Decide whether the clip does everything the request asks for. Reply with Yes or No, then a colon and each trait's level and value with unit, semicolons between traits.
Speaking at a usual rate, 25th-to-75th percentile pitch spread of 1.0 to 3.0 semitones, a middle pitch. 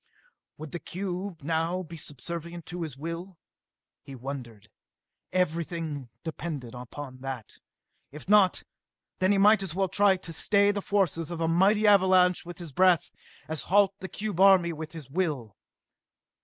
No: average, 155 wpm; average, 3.8 semitones; medium, 170 Hz